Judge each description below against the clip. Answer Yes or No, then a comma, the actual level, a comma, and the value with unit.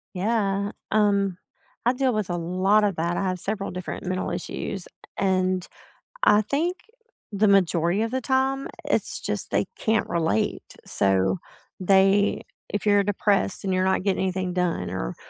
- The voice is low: No, high, 195 Hz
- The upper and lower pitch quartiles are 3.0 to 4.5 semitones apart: No, narrow, 2.5 semitones